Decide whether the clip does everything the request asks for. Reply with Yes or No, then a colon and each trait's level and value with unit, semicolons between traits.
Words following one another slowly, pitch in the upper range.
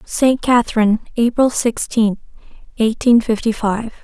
Yes: slow, 105 wpm; high, 230 Hz